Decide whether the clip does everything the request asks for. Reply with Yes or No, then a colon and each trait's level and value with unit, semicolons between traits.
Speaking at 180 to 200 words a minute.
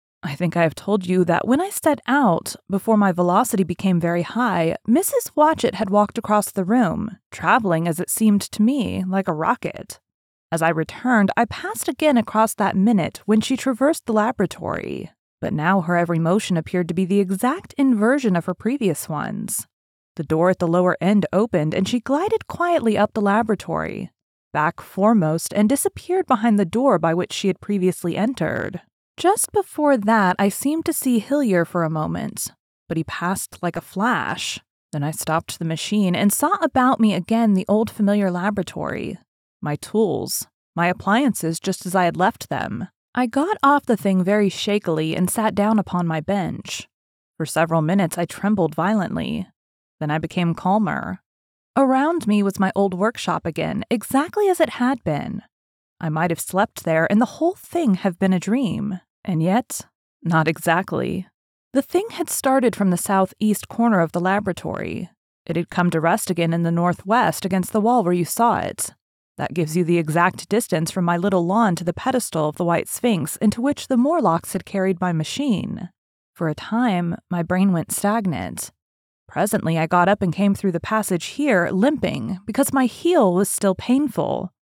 Yes: average, 185 wpm